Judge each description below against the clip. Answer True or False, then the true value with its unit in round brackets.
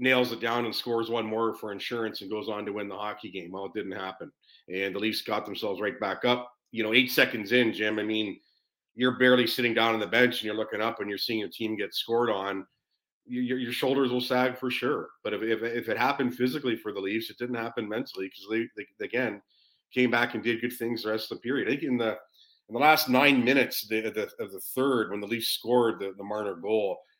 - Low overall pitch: True (115 Hz)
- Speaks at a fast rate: True (245 wpm)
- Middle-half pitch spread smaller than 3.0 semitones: True (2.6 semitones)